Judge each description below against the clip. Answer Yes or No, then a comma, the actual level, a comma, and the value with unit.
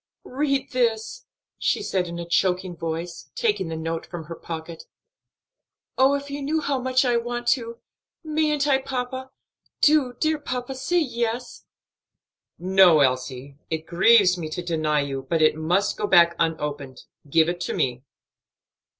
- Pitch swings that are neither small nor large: No, wide, 8.1 semitones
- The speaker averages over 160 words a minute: No, average, 155 wpm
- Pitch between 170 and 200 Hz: Yes, high, 190 Hz